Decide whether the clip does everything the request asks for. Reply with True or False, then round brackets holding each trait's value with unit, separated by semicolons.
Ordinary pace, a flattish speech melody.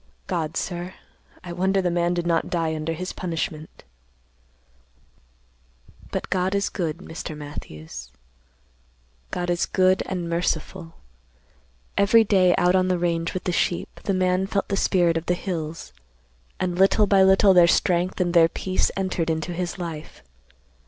True (150 wpm; 2.0 semitones)